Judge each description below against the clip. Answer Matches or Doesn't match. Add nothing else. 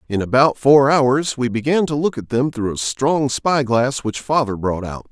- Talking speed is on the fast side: Matches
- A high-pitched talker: Doesn't match